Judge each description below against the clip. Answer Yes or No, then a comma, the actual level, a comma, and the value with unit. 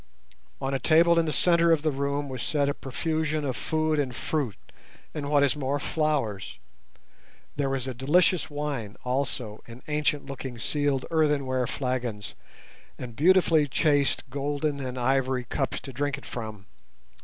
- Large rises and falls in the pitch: No, average, 2.8 semitones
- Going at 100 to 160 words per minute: Yes, average, 155 wpm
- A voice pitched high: No, medium, 140 Hz